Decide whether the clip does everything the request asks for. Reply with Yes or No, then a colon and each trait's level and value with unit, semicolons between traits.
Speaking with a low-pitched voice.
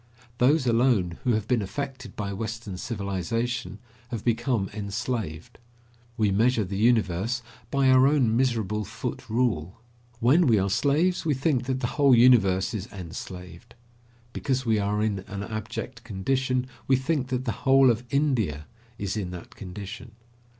Yes: low, 115 Hz